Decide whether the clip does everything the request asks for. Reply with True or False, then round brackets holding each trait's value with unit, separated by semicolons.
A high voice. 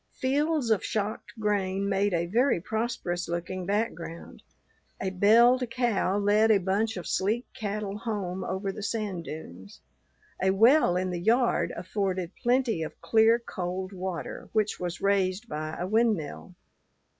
True (200 Hz)